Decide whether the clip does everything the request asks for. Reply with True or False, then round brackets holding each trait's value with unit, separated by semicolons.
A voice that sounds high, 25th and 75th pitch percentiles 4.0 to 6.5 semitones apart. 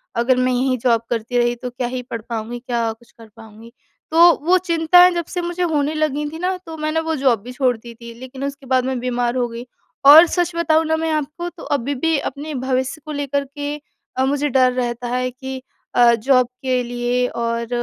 True (260 Hz; 4.3 semitones)